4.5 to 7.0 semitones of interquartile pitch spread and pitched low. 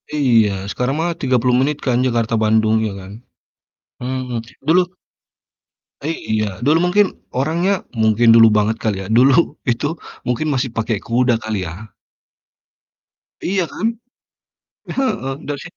Yes: average, 4.9 semitones; low, 125 Hz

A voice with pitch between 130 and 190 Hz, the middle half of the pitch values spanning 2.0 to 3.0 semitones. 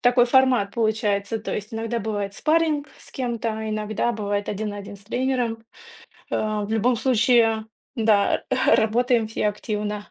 No: high, 220 Hz; narrow, 2.4 semitones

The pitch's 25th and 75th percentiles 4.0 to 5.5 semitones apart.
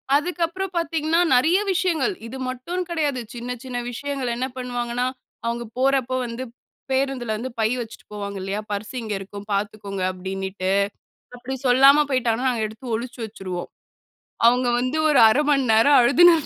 Yes: average, 4.4 semitones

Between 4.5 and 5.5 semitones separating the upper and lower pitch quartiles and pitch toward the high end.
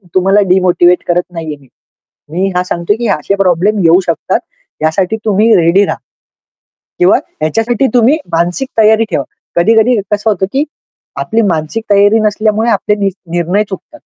No: average, 4.0 semitones; high, 195 Hz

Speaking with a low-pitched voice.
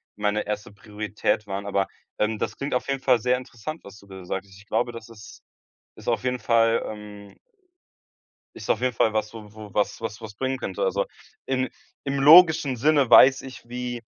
Yes: low, 115 Hz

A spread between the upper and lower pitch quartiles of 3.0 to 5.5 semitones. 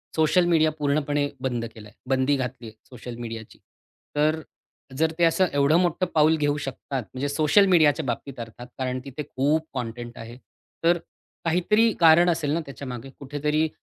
Yes: average, 3.9 semitones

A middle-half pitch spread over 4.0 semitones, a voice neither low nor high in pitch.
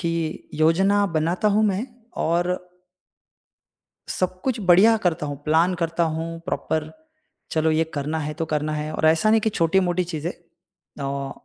No: average, 2.8 semitones; medium, 165 Hz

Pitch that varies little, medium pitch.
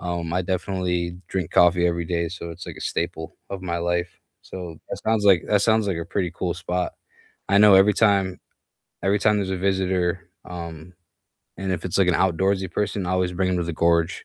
No: narrow, 1.9 semitones; very low, 90 Hz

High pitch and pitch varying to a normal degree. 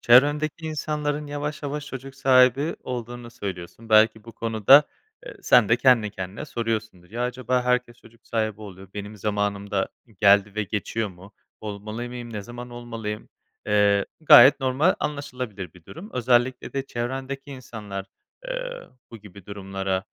No: low, 120 Hz; average, 4.2 semitones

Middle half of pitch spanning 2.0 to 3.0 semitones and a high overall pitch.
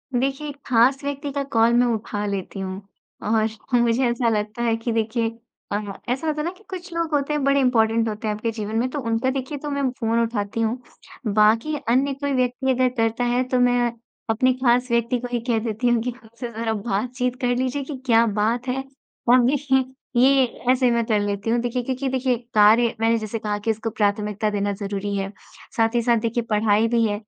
Yes: average, 2.7 semitones; high, 235 Hz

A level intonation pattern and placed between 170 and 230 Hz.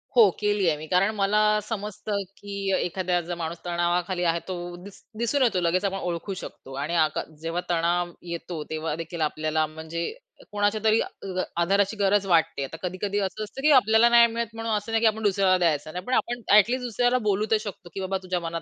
No: average, 3.9 semitones; high, 190 Hz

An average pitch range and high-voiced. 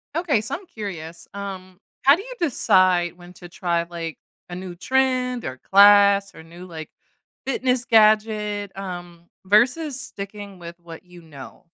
Yes: average, 4.3 semitones; high, 195 Hz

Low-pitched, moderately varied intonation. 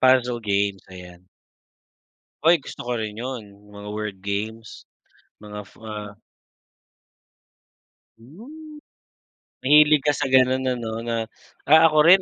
No: low, 120 Hz; wide, 5.9 semitones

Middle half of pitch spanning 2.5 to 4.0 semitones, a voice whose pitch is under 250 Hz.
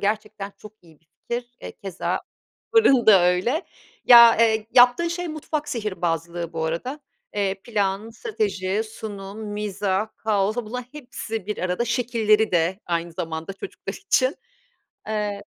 Yes: average, 3.7 semitones; high, 210 Hz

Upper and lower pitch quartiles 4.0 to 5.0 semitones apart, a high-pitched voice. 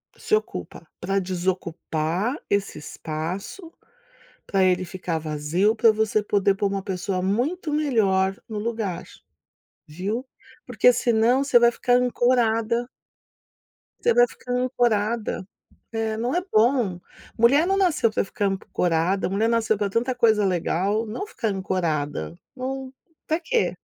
Yes: average, 4.6 semitones; high, 215 Hz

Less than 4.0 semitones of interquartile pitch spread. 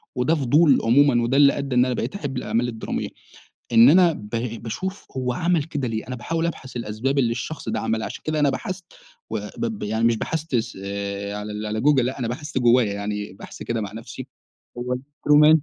No: average, 4.7 semitones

